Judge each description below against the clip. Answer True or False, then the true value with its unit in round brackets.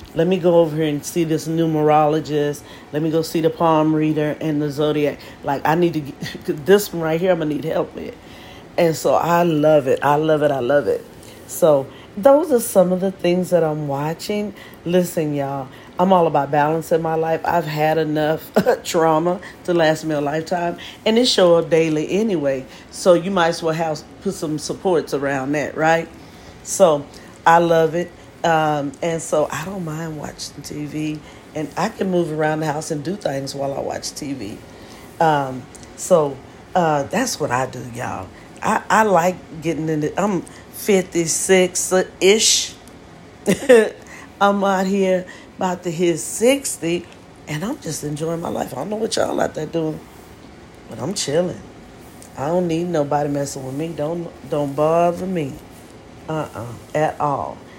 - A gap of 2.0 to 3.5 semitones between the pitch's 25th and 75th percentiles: True (2.9 semitones)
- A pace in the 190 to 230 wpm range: False (180 wpm)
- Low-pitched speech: False (160 Hz)